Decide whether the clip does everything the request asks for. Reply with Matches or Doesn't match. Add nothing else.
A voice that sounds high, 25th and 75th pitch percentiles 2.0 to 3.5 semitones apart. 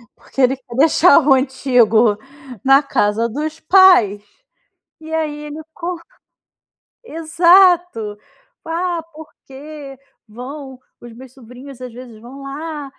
Doesn't match